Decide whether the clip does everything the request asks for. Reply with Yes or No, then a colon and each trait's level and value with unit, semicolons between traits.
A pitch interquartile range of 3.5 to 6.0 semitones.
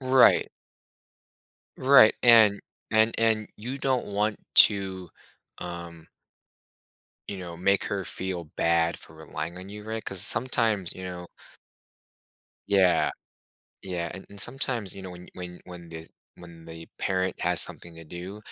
Yes: average, 3.8 semitones